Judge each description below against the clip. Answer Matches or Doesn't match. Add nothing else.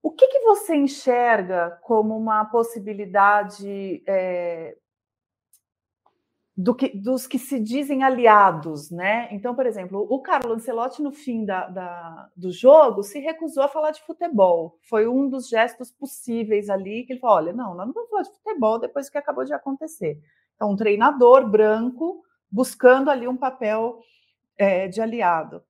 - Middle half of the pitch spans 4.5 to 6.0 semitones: Matches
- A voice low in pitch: Doesn't match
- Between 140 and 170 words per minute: Matches